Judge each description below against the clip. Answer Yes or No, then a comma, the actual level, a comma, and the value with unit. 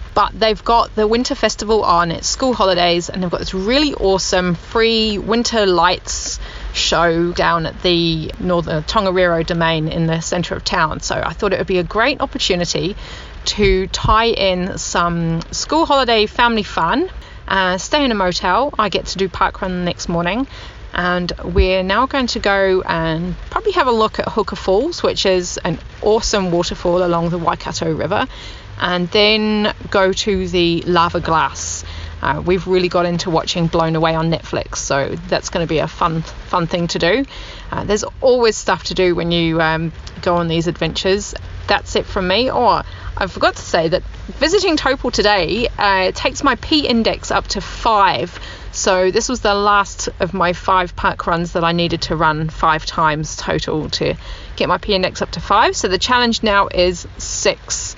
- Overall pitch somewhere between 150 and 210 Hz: Yes, medium, 185 Hz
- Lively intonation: No, average, 4.1 semitones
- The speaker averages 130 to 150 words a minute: No, average, 185 wpm